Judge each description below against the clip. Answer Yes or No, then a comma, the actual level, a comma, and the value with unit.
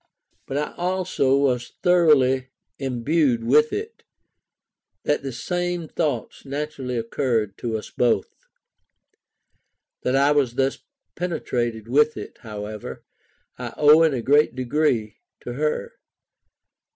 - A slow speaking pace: Yes, slow, 120 wpm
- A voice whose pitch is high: No, low, 135 Hz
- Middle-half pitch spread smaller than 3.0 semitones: No, average, 4.4 semitones